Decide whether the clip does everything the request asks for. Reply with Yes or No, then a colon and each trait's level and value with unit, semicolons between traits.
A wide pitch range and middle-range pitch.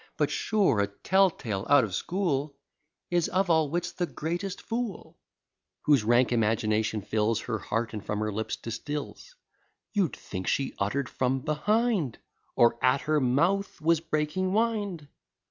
Yes: wide, 7.9 semitones; medium, 145 Hz